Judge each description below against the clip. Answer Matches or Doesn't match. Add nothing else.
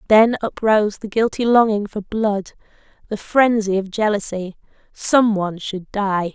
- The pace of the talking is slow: Matches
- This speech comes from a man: Doesn't match